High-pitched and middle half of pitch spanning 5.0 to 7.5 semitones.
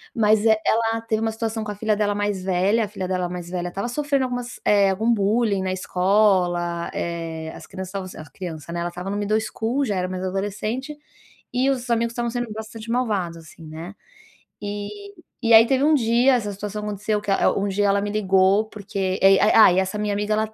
No: high, 205 Hz; average, 3.2 semitones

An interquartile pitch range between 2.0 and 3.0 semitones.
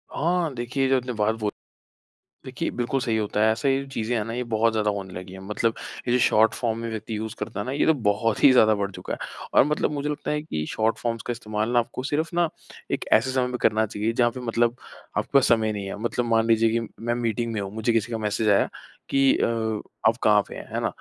Yes: narrow, 2.5 semitones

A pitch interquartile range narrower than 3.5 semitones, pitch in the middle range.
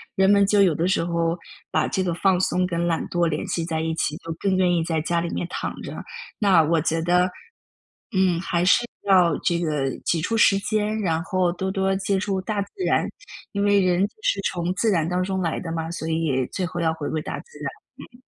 Yes: narrow, 2.6 semitones; medium, 175 Hz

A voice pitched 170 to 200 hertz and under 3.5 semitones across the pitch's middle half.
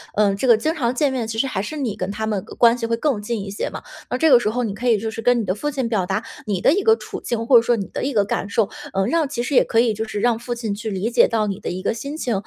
No: high, 230 Hz; average, 3.1 semitones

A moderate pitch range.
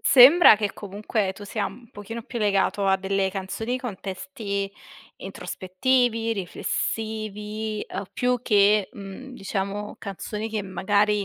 No: narrow, 2.3 semitones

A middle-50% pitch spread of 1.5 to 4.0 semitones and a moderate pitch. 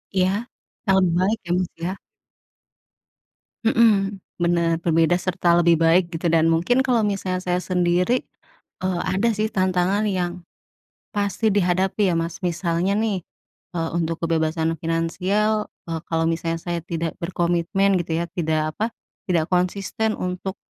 Yes: average, 2.8 semitones; medium, 180 Hz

